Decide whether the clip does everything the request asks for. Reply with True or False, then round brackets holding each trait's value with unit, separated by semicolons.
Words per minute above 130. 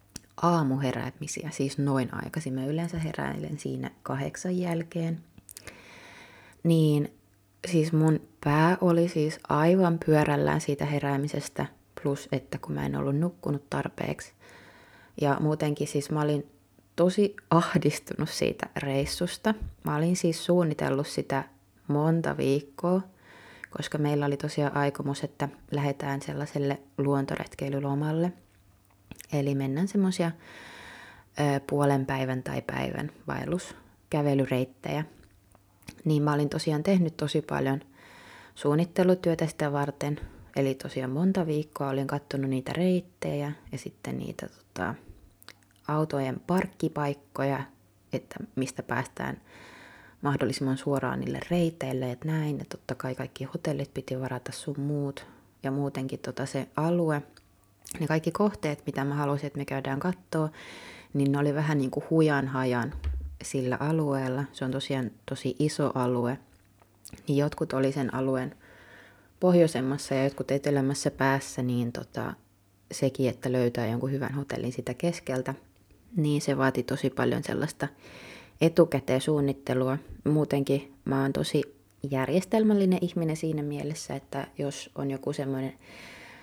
False (120 wpm)